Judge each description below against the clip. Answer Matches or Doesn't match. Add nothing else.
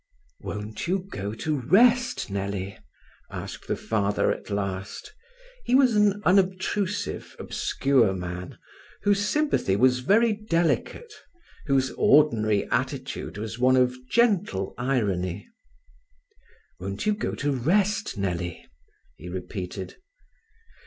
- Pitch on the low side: Matches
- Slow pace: Matches